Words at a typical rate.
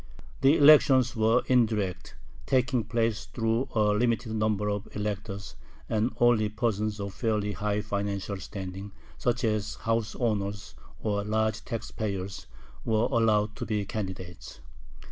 No: slow, 130 wpm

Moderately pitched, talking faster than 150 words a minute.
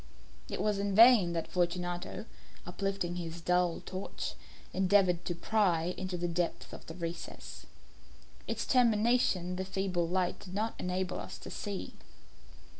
No: medium, 180 Hz; average, 140 wpm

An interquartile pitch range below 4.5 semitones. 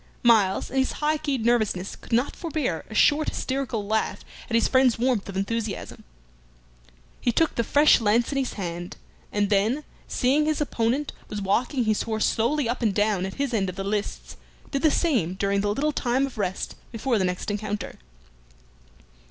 No: average, 4.8 semitones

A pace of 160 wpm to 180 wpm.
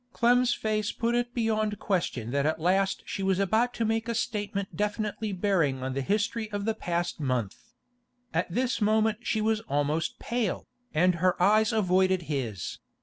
Yes: average, 170 wpm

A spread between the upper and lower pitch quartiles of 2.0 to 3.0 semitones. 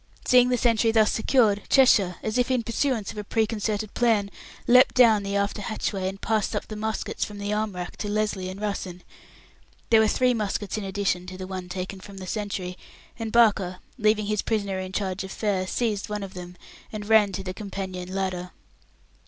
Yes: narrow, 2.6 semitones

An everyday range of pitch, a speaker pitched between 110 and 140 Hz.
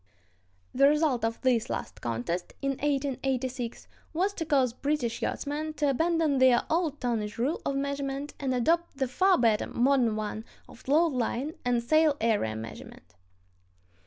No: average, 4.0 semitones; very high, 270 Hz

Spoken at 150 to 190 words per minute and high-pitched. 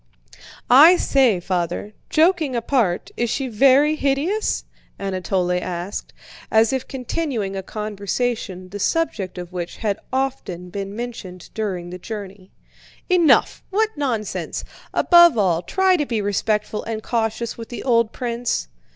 No: slow, 135 wpm; high, 225 Hz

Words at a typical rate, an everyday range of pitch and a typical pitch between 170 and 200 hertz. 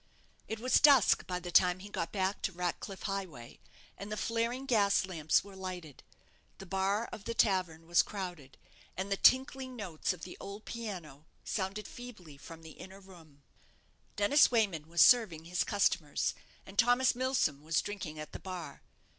Yes: average, 170 wpm; average, 4.2 semitones; high, 190 Hz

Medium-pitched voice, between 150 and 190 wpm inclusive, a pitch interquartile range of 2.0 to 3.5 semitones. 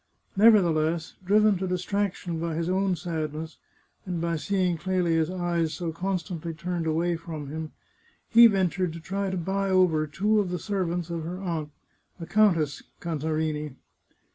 Yes: medium, 175 Hz; average, 155 wpm; average, 2.7 semitones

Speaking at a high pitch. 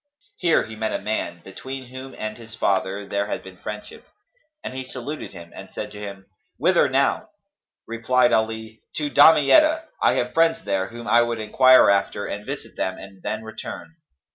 No: low, 110 Hz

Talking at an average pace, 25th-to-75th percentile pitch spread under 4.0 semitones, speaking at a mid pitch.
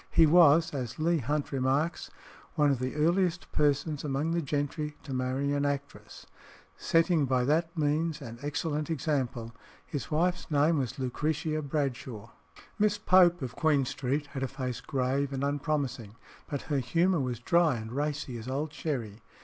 Yes: average, 160 wpm; average, 3.2 semitones; medium, 145 Hz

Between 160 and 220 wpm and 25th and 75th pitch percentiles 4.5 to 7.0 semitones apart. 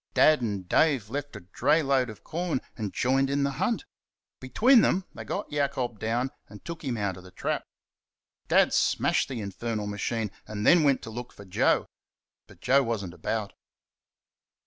Yes: average, 180 wpm; wide, 5.4 semitones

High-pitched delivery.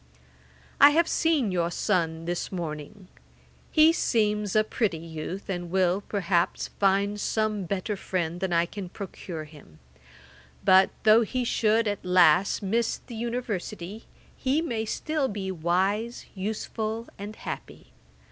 Yes: high, 200 Hz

